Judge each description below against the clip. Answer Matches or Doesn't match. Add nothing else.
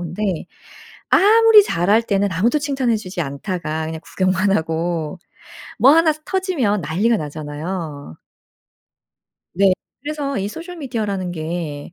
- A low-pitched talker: Doesn't match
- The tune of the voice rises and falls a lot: Matches